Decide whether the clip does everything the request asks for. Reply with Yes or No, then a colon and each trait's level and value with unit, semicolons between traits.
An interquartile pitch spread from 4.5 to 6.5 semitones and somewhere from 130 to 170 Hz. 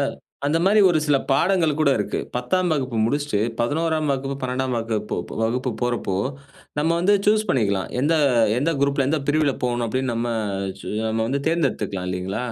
Yes: average, 4.9 semitones; low, 135 Hz